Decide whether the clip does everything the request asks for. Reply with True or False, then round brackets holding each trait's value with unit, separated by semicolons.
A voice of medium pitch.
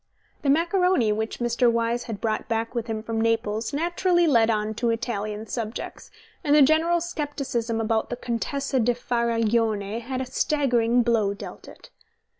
False (235 Hz)